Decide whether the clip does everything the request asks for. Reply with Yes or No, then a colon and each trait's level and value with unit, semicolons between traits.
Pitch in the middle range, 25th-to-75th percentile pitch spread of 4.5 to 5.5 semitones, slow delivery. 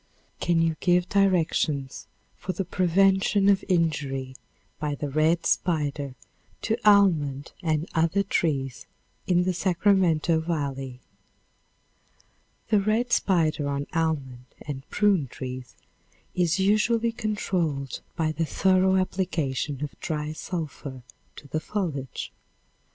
Yes: medium, 165 Hz; average, 4.9 semitones; slow, 110 wpm